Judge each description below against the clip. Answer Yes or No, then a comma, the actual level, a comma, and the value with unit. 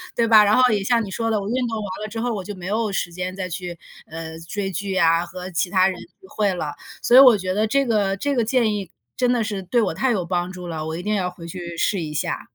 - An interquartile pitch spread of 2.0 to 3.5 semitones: No, average, 4.0 semitones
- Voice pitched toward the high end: Yes, high, 195 Hz